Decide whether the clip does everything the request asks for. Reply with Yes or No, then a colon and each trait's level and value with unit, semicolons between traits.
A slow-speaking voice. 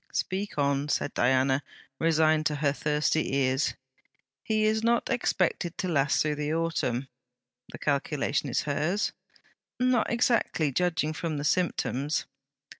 Yes: slow, 130 wpm